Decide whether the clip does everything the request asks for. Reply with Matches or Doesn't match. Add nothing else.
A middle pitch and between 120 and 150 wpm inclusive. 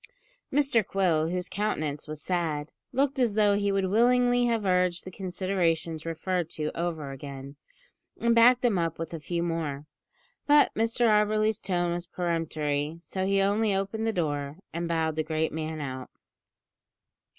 Doesn't match